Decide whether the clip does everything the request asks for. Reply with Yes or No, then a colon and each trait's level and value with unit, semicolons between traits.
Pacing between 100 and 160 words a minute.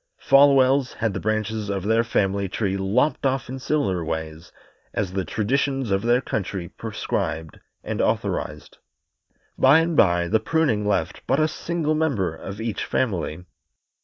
Yes: average, 150 wpm